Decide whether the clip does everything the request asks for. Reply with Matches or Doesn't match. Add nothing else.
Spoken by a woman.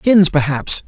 Doesn't match